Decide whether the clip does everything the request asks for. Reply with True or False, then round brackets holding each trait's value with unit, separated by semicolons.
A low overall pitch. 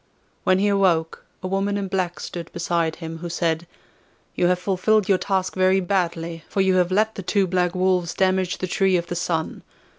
False (185 Hz)